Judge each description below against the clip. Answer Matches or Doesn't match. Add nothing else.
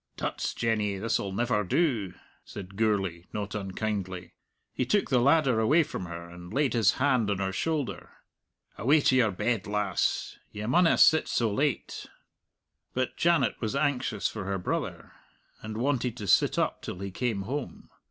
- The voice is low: Matches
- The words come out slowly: Doesn't match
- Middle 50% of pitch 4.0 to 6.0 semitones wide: Matches